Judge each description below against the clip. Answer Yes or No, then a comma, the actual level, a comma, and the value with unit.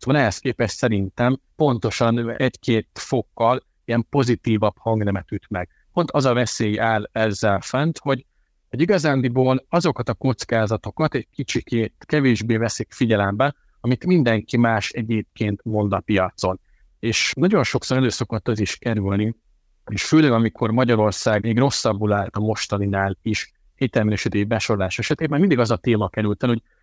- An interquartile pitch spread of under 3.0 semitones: No, average, 3.4 semitones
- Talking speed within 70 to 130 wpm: No, average, 145 wpm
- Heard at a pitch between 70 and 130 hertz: Yes, low, 115 Hz